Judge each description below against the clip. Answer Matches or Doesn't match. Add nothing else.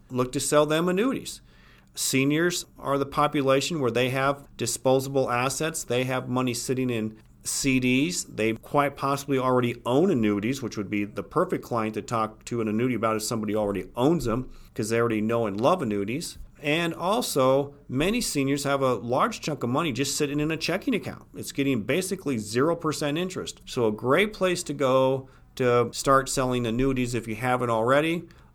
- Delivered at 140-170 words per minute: Doesn't match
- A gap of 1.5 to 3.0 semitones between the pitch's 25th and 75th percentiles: Doesn't match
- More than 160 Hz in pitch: Doesn't match